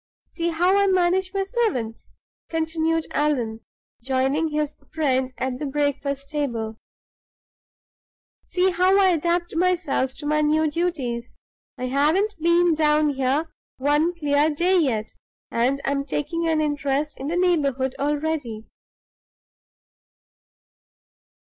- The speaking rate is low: Yes, slow, 115 wpm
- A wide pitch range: No, average, 3.9 semitones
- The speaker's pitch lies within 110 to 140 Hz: No, very high, 300 Hz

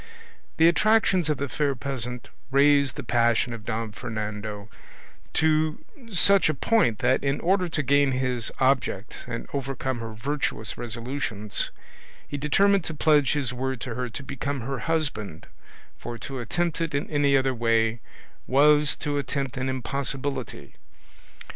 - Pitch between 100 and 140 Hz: Yes, low, 135 Hz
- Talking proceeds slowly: No, average, 150 wpm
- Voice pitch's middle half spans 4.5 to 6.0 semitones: No, average, 3.8 semitones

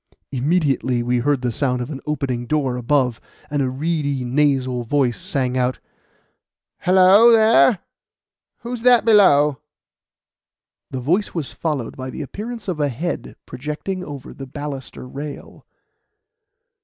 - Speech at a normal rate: No, slow, 130 wpm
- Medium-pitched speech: Yes, medium, 145 Hz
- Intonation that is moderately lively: Yes, average, 5.0 semitones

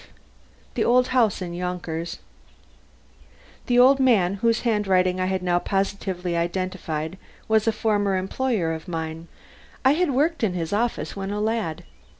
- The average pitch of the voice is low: No, high, 195 Hz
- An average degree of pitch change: Yes, average, 4.4 semitones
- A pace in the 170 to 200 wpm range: No, average, 150 wpm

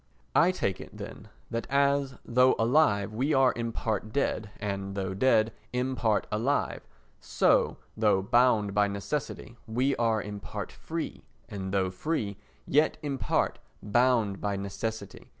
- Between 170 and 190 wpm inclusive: No, average, 150 wpm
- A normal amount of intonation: Yes, average, 4.4 semitones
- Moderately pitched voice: No, low, 110 Hz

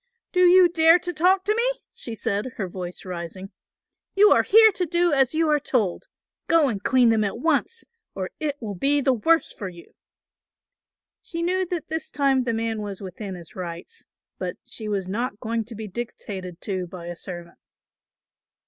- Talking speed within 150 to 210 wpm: Yes, average, 185 wpm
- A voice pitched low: No, high, 235 Hz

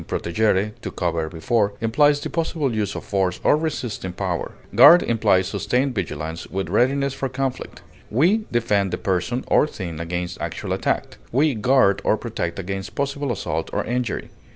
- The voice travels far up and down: Yes, wide, 6.3 semitones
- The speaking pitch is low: Yes, low, 110 Hz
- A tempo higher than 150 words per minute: Yes, average, 160 wpm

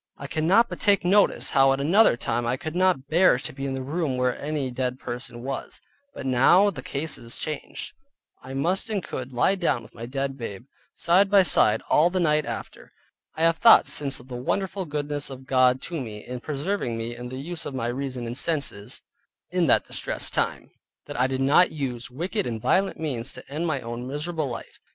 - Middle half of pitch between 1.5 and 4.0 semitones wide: No, average, 4.9 semitones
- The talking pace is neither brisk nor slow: No, fast, 210 wpm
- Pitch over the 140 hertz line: No, low, 135 Hz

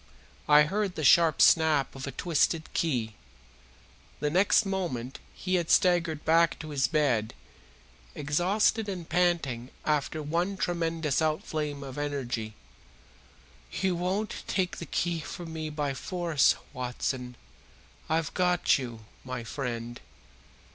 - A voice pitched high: No, medium, 155 Hz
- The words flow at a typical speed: No, slow, 125 wpm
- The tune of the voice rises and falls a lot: No, average, 4.3 semitones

